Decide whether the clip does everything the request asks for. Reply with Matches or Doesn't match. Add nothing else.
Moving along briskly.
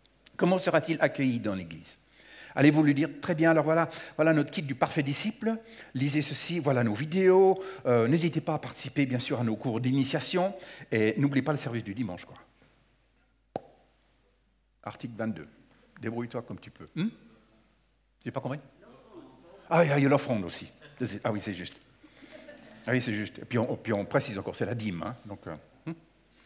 Doesn't match